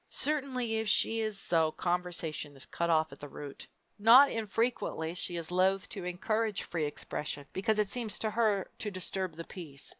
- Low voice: No, high, 190 Hz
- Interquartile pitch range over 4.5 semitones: Yes, average, 5.1 semitones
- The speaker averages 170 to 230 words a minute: Yes, average, 180 wpm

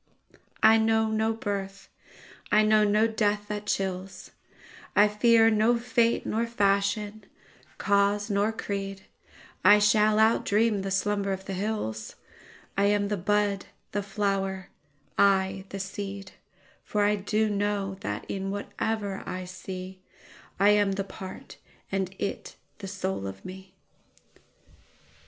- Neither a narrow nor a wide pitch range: No, narrow, 1.5 semitones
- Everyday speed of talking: No, slow, 120 wpm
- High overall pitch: Yes, high, 205 Hz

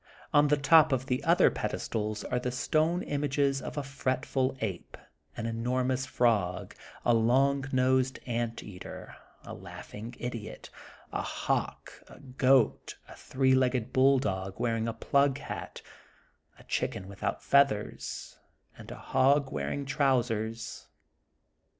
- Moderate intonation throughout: Yes, average, 3.2 semitones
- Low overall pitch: Yes, low, 130 Hz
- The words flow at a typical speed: No, slow, 130 wpm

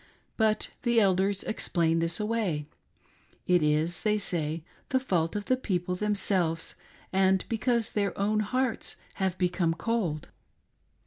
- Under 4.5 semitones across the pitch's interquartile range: Yes, average, 4.1 semitones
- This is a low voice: No, high, 190 Hz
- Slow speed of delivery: Yes, slow, 130 wpm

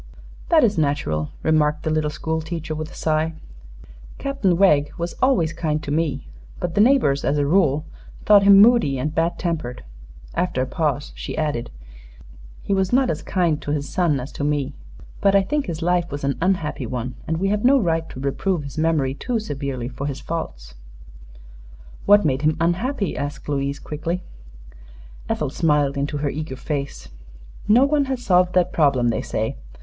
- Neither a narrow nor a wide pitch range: Yes, average, 4.5 semitones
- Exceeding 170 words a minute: Yes, average, 180 wpm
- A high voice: No, medium, 155 Hz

